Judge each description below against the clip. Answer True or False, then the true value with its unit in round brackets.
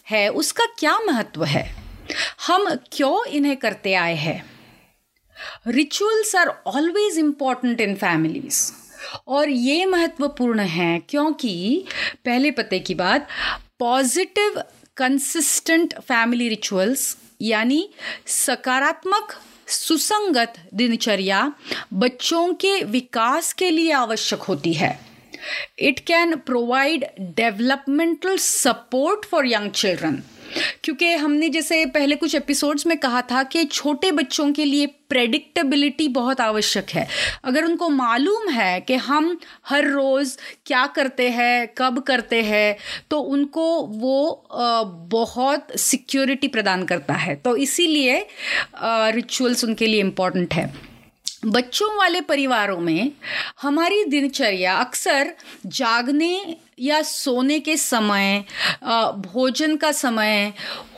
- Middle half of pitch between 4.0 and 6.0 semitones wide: True (5.4 semitones)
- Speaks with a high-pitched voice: True (270 Hz)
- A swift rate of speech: False (110 wpm)